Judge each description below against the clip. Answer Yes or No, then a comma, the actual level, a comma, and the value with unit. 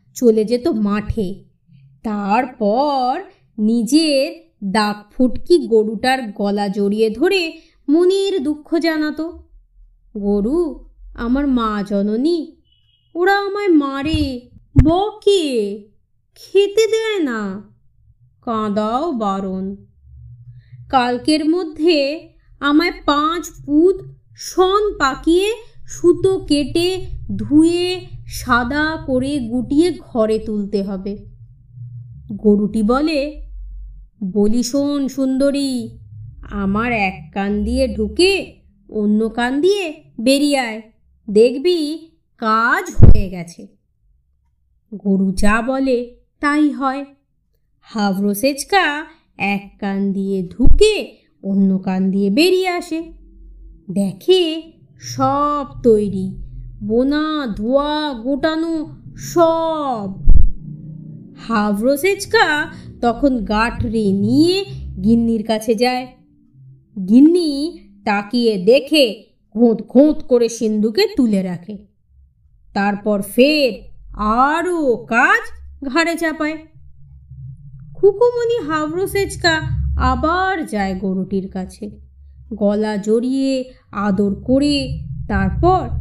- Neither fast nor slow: Yes, average, 80 wpm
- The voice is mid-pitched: No, high, 245 Hz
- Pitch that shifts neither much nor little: No, wide, 7.4 semitones